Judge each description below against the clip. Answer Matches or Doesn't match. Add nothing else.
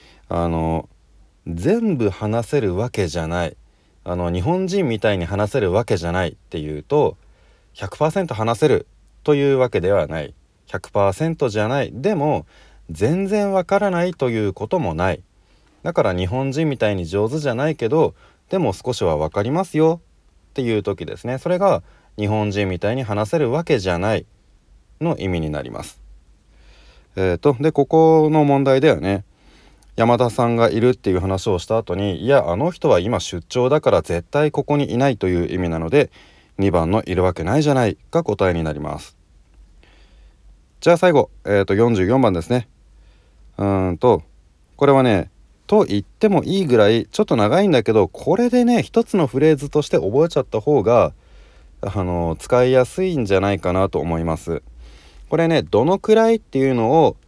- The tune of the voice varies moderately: Doesn't match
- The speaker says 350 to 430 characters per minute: Doesn't match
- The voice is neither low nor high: Doesn't match